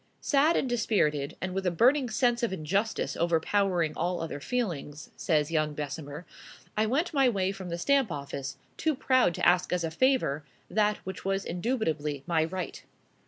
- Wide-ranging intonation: Yes, wide, 6.8 semitones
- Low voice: No, medium, 185 Hz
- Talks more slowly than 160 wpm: No, average, 170 wpm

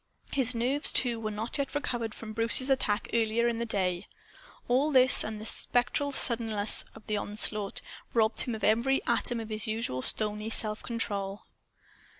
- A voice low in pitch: No, high, 225 Hz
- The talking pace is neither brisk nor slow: Yes, average, 165 wpm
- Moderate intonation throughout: No, narrow, 2.3 semitones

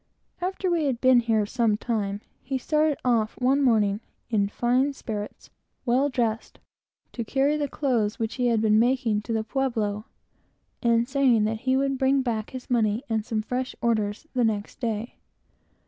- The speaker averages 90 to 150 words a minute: No, average, 165 wpm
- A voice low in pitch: No, high, 235 Hz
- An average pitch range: Yes, average, 3.5 semitones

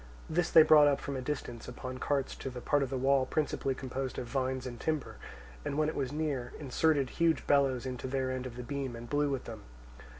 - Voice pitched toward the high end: No, low, 135 Hz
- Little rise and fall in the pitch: Yes, narrow, 2.2 semitones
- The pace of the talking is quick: Yes, fast, 230 wpm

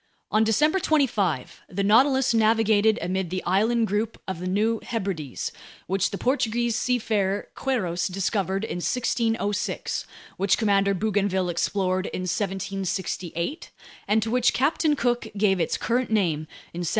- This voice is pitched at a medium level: No, high, 205 Hz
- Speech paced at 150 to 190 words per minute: No, average, 140 wpm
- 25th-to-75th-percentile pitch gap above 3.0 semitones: Yes, average, 3.5 semitones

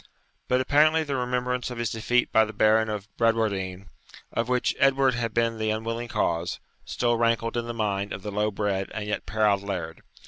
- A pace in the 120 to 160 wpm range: No, average, 195 wpm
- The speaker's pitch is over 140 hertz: No, low, 115 Hz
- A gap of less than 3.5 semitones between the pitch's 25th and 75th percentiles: Yes, average, 2.7 semitones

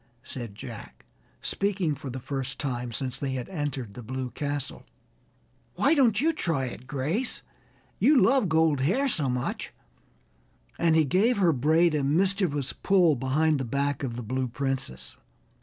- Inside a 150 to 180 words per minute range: Yes, average, 155 wpm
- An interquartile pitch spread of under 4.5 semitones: No, average, 5.1 semitones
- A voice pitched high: No, medium, 145 Hz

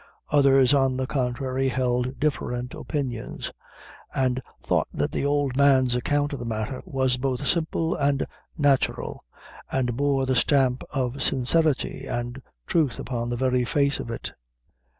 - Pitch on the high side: No, low, 130 Hz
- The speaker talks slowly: No, average, 145 wpm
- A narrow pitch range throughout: Yes, narrow, 2.2 semitones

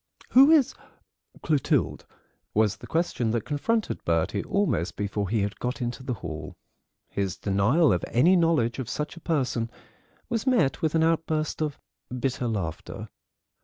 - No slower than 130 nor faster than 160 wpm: Yes, average, 150 wpm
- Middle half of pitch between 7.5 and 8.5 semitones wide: Yes, wide, 7.9 semitones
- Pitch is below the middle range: Yes, low, 130 Hz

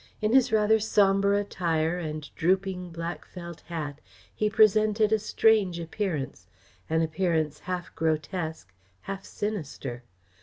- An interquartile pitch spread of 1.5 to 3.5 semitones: No, average, 4.5 semitones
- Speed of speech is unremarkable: No, slow, 120 wpm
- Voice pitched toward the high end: No, medium, 180 Hz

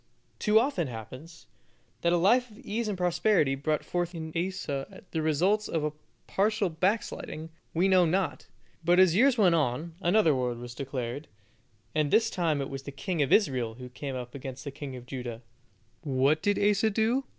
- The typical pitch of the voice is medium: Yes, medium, 165 Hz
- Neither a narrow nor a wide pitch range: No, wide, 6.2 semitones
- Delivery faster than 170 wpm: Yes, average, 180 wpm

